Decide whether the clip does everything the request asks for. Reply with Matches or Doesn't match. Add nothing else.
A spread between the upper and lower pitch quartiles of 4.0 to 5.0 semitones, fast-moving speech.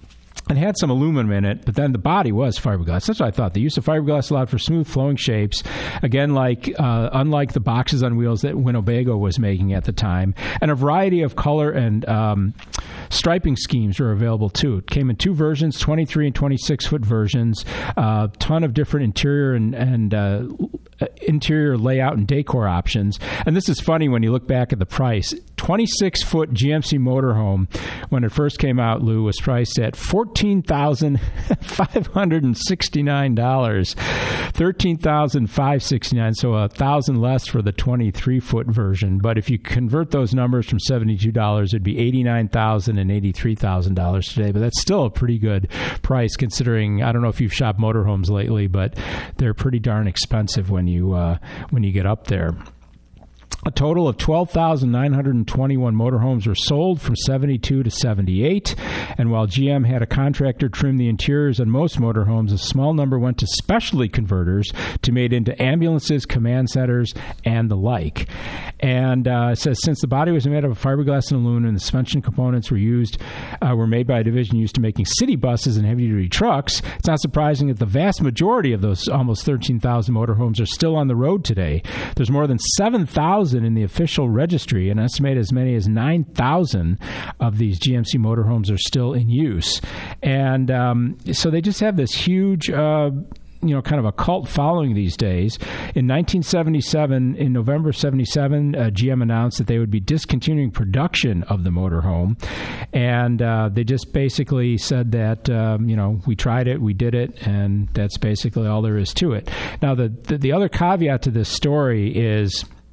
Doesn't match